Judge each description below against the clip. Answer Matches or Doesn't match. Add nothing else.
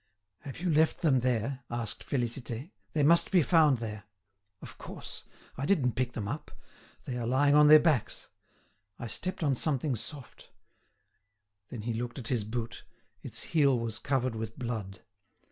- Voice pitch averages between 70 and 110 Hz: Doesn't match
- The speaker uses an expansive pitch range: Doesn't match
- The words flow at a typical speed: Matches